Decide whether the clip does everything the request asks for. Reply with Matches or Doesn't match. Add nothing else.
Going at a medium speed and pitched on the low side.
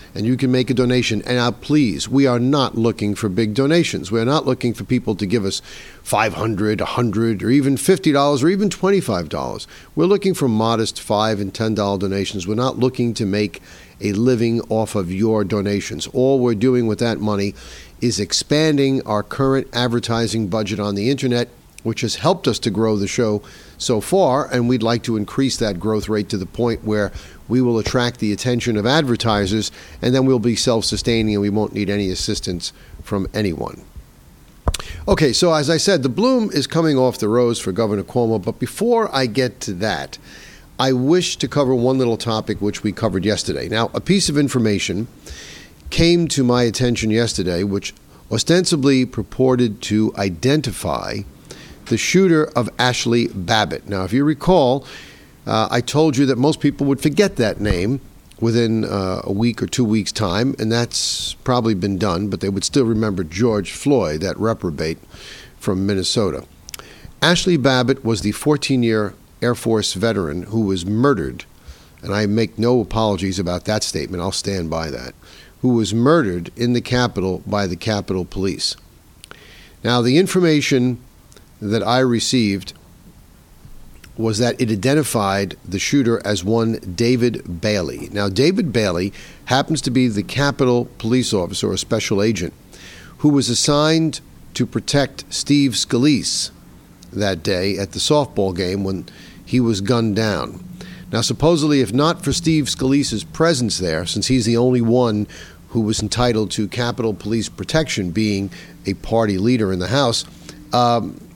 Matches